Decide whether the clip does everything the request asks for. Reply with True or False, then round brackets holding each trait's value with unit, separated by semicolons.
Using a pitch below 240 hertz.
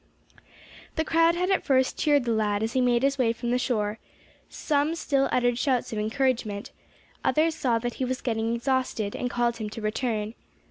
False (245 Hz)